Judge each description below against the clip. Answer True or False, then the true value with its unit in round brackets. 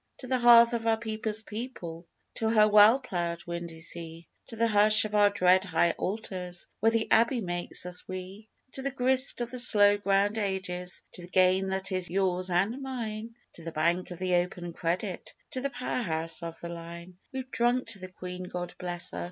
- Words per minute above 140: True (200 wpm)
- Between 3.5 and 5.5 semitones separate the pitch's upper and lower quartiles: True (4.2 semitones)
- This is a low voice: False (190 Hz)